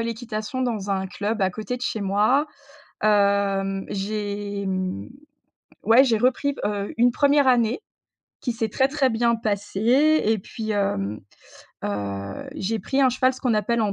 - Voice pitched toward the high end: Yes, high, 215 Hz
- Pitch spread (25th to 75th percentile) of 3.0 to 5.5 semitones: Yes, average, 3.7 semitones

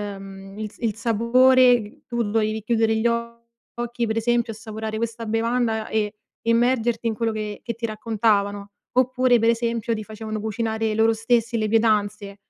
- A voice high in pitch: Yes, high, 225 Hz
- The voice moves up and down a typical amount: No, narrow, 1.4 semitones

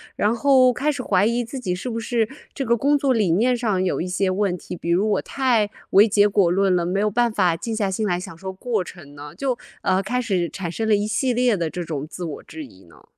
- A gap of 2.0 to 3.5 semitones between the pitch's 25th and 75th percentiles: No, average, 4.8 semitones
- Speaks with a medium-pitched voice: No, high, 205 Hz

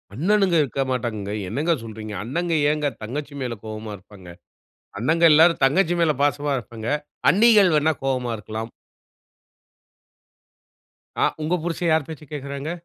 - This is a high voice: No, medium, 140 Hz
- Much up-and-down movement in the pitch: Yes, wide, 6.2 semitones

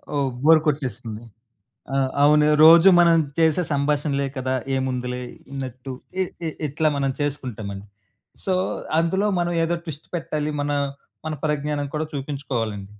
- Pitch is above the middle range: No, medium, 145 Hz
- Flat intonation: No, average, 3.2 semitones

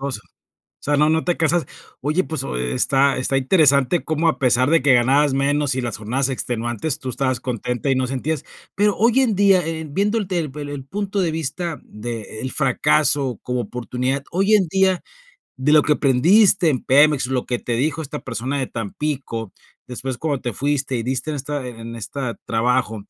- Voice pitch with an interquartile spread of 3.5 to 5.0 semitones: Yes, average, 4.1 semitones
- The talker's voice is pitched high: No, medium, 140 Hz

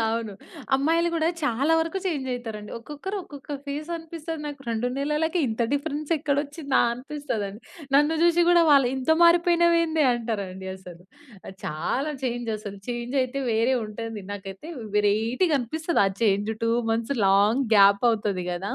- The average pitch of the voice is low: No, very high, 265 Hz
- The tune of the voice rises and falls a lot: Yes, wide, 6.2 semitones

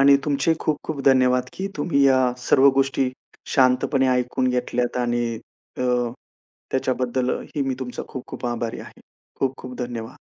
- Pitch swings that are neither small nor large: No, narrow, 1.7 semitones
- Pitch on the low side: Yes, low, 130 Hz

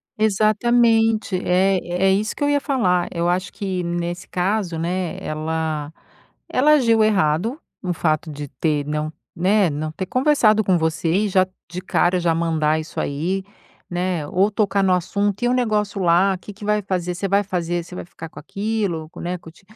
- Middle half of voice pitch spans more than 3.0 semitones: Yes, average, 4.0 semitones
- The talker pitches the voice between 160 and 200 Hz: Yes, medium, 185 Hz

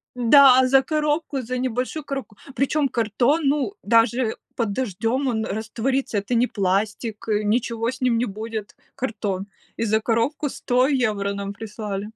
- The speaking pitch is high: Yes, high, 230 Hz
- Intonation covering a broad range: No, average, 3.5 semitones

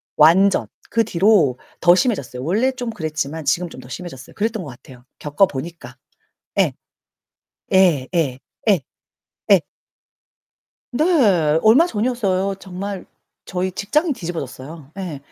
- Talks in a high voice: No, medium, 180 Hz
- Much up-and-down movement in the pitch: Yes, wide, 5.8 semitones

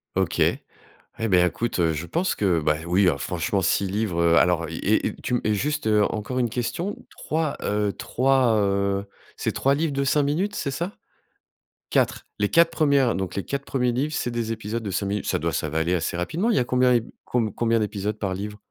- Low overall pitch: Yes, low, 110 Hz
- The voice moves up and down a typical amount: No, wide, 6.1 semitones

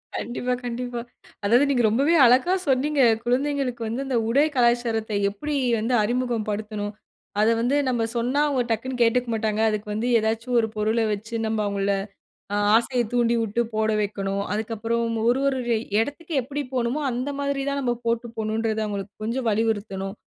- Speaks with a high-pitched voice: Yes, high, 235 Hz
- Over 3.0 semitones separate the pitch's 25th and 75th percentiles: No, average, 2.7 semitones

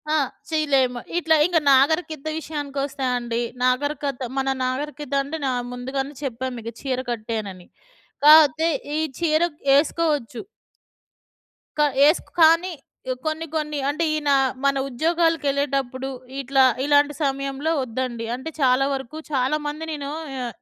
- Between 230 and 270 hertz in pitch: No, very high, 280 Hz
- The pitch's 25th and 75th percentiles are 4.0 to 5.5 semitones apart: No, average, 3.1 semitones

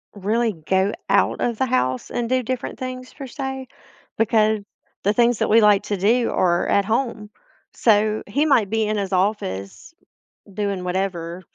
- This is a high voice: Yes, high, 210 Hz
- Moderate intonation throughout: Yes, average, 3.9 semitones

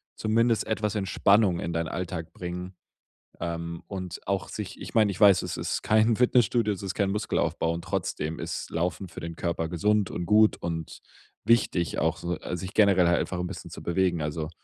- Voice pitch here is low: Yes, very low, 90 Hz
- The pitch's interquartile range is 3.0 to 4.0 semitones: Yes, average, 3.7 semitones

